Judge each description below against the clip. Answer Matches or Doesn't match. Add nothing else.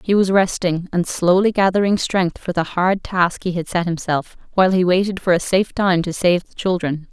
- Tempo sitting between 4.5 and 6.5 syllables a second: Matches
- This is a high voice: Doesn't match